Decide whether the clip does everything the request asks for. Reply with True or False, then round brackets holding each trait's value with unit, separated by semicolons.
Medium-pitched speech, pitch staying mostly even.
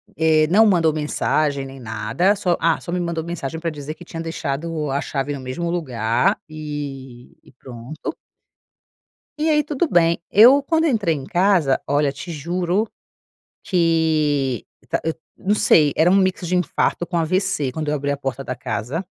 False (160 Hz; 4.2 semitones)